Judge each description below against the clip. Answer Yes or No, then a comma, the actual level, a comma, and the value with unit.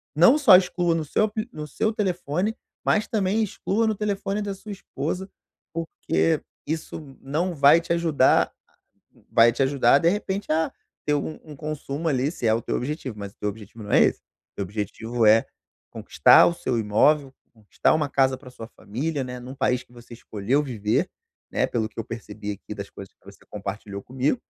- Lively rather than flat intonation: Yes, wide, 6.9 semitones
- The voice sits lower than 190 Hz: Yes, medium, 140 Hz